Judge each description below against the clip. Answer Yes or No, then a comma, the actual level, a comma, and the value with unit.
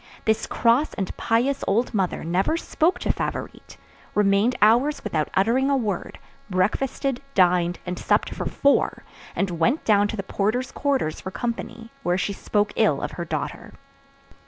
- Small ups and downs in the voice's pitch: No, average, 5.1 semitones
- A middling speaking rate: Yes, average, 160 wpm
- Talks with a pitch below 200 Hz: No, high, 215 Hz